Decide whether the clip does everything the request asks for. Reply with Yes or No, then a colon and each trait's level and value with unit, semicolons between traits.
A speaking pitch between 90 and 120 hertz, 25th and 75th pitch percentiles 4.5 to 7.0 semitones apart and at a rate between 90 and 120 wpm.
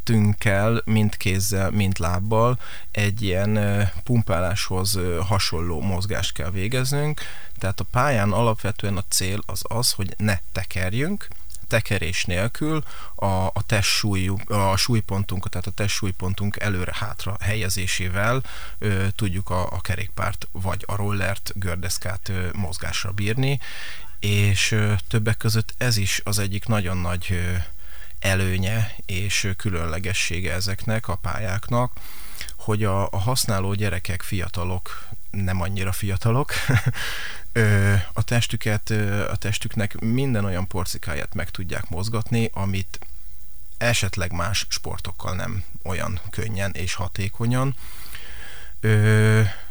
No: low, 100 Hz; average, 2.7 semitones; slow, 105 wpm